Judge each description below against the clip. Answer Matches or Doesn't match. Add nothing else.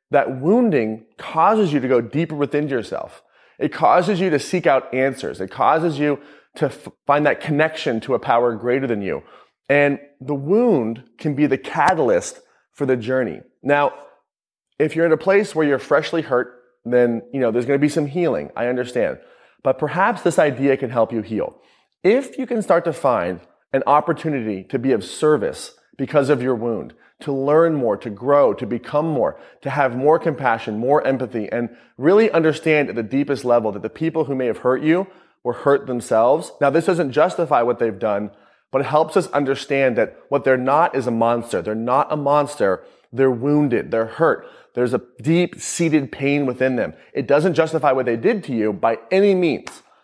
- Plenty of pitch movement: Doesn't match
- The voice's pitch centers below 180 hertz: Matches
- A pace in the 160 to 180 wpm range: Doesn't match